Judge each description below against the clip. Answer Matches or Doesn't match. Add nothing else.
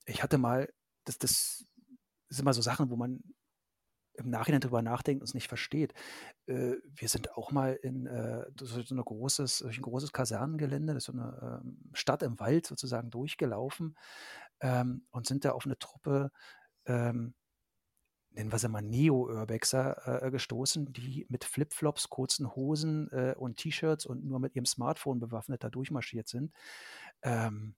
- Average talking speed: Matches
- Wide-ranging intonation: Doesn't match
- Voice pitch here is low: Matches